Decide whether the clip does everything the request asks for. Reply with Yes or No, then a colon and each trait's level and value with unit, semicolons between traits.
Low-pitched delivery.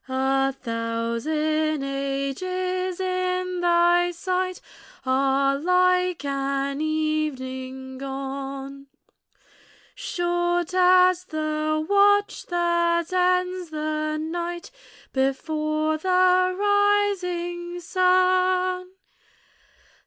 No: very high, 340 Hz